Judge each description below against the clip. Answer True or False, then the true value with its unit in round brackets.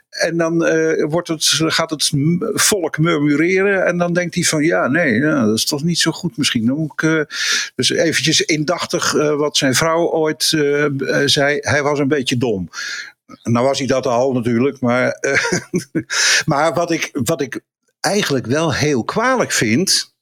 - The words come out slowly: False (180 wpm)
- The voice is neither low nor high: True (155 Hz)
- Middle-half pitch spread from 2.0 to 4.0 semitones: True (3.0 semitones)